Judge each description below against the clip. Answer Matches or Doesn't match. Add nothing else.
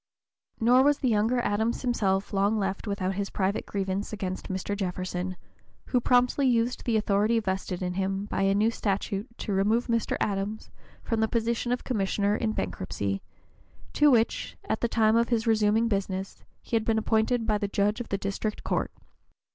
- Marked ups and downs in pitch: Doesn't match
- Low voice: Doesn't match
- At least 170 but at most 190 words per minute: Matches